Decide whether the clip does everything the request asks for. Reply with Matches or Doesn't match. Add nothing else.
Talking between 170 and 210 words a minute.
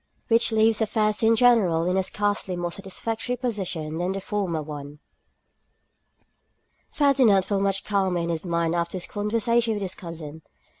Doesn't match